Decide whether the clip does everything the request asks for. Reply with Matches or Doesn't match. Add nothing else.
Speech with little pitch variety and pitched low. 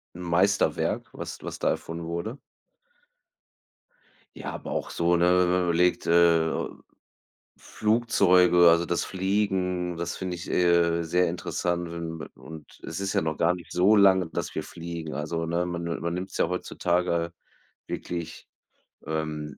Matches